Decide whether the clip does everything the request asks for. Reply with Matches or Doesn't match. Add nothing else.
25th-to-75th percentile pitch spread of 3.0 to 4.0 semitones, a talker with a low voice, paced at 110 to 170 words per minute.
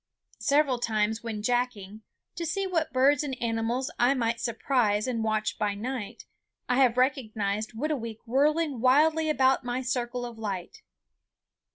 Doesn't match